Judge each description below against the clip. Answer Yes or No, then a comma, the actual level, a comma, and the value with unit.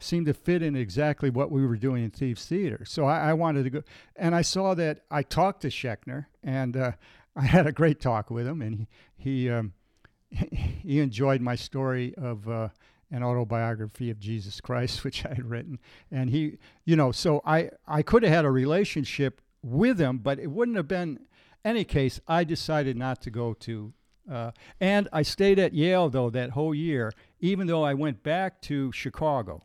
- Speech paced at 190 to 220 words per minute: Yes, average, 200 wpm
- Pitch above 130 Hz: Yes, medium, 140 Hz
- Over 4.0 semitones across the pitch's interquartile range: Yes, average, 4.6 semitones